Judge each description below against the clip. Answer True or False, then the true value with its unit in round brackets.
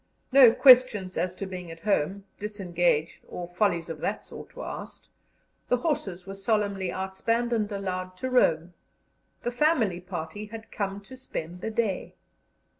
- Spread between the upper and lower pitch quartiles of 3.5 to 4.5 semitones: True (4.0 semitones)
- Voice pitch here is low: False (195 Hz)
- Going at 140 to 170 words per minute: True (155 wpm)